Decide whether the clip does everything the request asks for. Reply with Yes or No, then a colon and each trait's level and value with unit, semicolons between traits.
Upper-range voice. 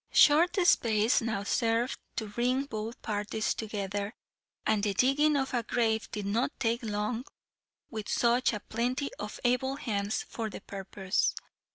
Yes: high, 225 Hz